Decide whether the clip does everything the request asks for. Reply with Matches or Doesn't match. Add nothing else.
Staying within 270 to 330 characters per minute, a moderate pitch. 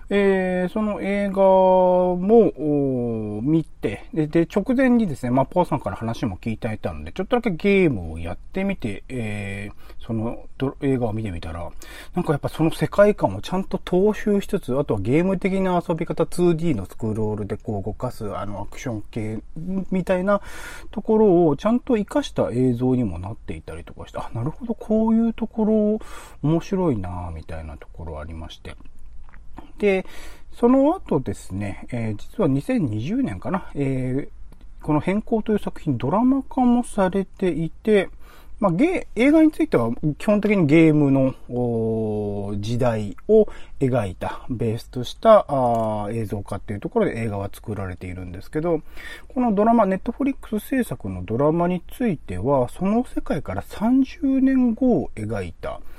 Matches